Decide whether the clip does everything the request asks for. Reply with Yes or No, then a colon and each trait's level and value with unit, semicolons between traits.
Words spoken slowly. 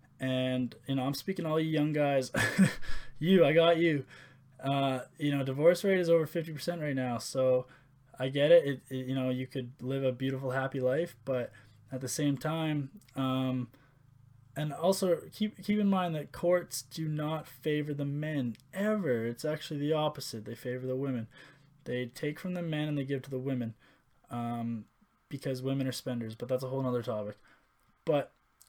No: average, 190 wpm